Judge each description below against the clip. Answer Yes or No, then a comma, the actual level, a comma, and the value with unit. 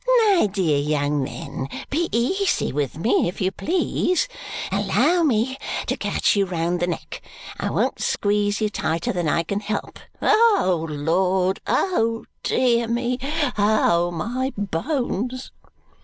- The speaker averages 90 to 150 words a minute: Yes, slow, 135 wpm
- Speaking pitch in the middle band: No, high, 205 Hz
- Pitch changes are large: Yes, wide, 6.8 semitones